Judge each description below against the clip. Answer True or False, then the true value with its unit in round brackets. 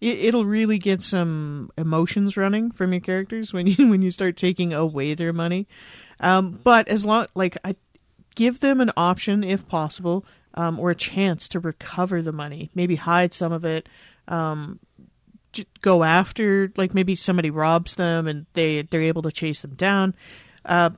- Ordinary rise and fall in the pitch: True (3.0 semitones)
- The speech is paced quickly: False (170 wpm)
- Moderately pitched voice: True (180 Hz)